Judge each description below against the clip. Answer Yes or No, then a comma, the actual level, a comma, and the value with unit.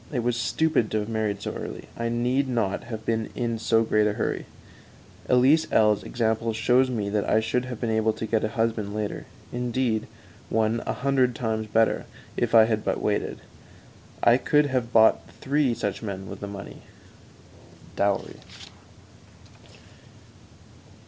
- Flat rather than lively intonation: Yes, narrow, 2.1 semitones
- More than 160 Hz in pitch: No, low, 115 Hz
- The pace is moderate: Yes, average, 160 wpm